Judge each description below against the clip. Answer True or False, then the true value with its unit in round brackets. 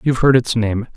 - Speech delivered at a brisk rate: True (250 wpm)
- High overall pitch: False (120 Hz)